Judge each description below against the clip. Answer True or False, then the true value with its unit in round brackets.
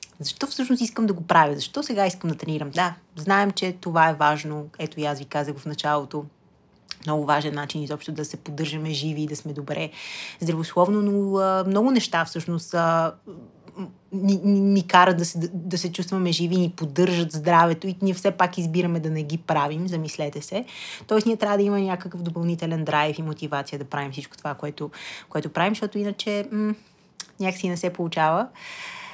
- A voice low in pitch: False (170 Hz)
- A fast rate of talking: True (185 wpm)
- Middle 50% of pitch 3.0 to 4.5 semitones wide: True (4.1 semitones)